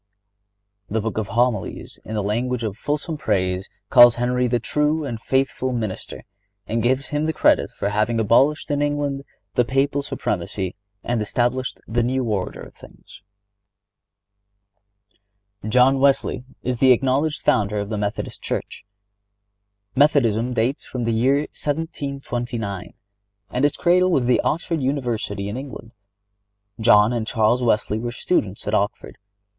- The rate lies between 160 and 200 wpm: No, average, 145 wpm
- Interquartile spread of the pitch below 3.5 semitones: No, average, 4.5 semitones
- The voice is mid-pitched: No, low, 120 Hz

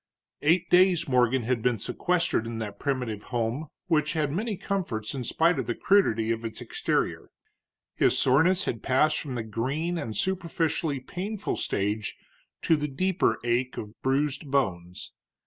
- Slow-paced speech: No, average, 155 wpm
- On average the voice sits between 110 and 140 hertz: Yes, low, 135 Hz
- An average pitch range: No, wide, 6.6 semitones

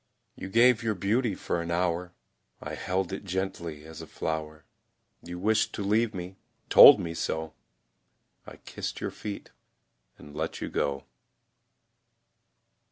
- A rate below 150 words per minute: Yes, average, 140 wpm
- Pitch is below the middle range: Yes, very low, 90 Hz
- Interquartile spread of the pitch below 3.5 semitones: No, average, 4.0 semitones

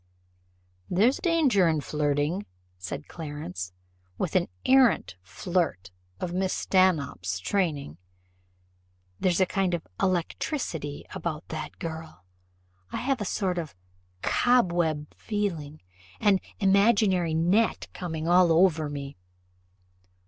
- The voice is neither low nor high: Yes, medium, 170 Hz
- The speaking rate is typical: No, slow, 105 wpm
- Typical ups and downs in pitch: Yes, average, 4.5 semitones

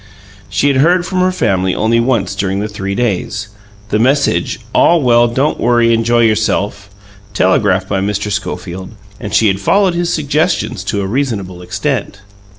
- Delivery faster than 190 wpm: No, average, 160 wpm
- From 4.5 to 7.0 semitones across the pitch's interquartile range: Yes, average, 5.3 semitones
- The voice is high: No, low, 110 Hz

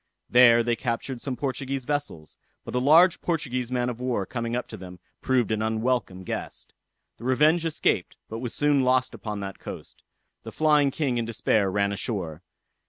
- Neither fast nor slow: Yes, average, 175 wpm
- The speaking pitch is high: No, low, 125 Hz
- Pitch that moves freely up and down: No, average, 3.6 semitones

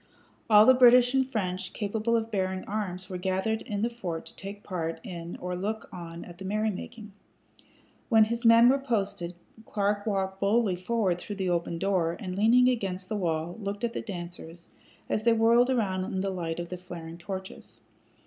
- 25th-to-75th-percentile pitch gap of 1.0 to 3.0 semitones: No, average, 3.6 semitones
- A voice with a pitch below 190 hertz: No, high, 195 Hz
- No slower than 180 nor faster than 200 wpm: Yes, average, 185 wpm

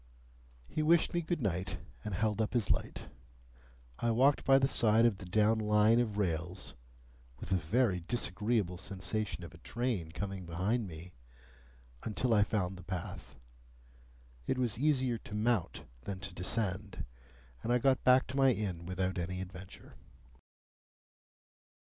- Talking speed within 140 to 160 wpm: Yes, average, 150 wpm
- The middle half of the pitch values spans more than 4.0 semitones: Yes, average, 4.5 semitones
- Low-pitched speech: Yes, low, 105 Hz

